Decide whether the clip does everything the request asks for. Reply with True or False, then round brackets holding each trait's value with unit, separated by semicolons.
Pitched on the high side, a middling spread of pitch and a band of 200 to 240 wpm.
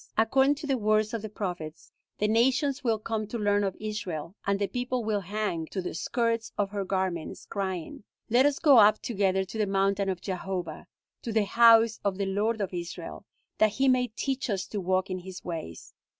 True (205 Hz; 3.3 semitones; 205 wpm)